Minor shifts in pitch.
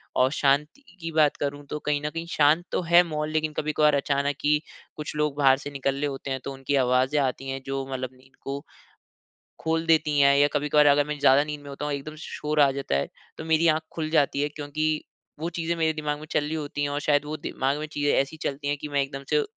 Yes: narrow, 1.8 semitones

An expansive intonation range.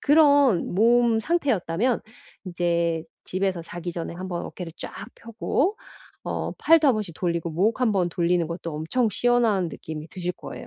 Yes: wide, 6.0 semitones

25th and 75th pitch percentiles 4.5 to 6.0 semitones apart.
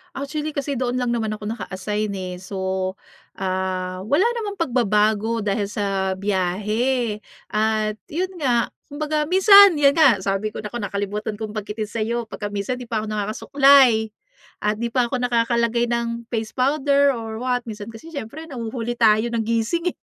No: average, 3.6 semitones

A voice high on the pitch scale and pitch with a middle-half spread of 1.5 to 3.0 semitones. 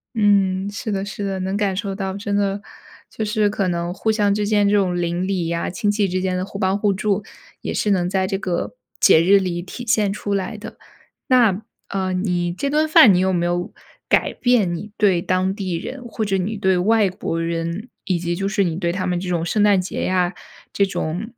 Yes: high, 195 Hz; narrow, 2.4 semitones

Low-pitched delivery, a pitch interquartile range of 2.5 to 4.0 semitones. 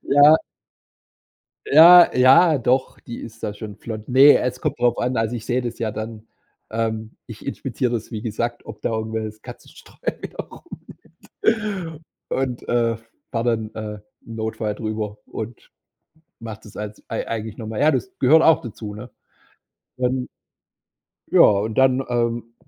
Yes: low, 115 Hz; average, 2.8 semitones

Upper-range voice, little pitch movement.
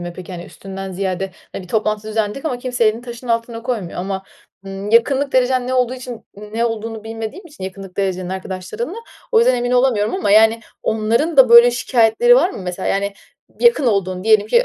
No: high, 225 Hz; average, 4.2 semitones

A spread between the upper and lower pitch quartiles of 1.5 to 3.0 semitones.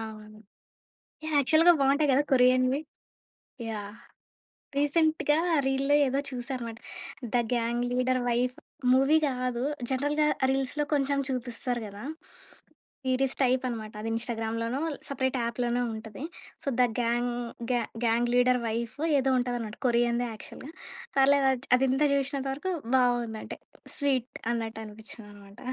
Yes: narrow, 2.6 semitones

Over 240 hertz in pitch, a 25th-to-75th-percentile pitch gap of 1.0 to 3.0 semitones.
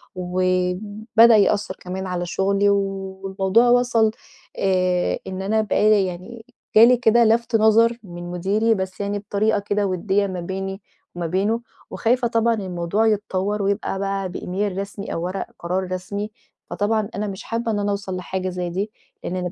No: high, 200 Hz; average, 2.7 semitones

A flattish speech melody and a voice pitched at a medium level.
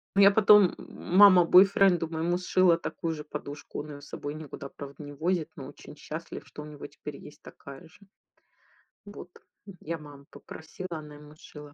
No: average, 3.7 semitones; medium, 160 Hz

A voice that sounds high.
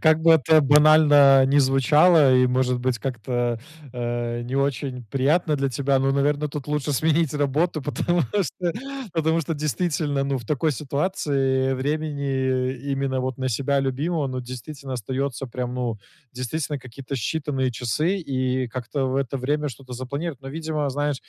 No: low, 135 Hz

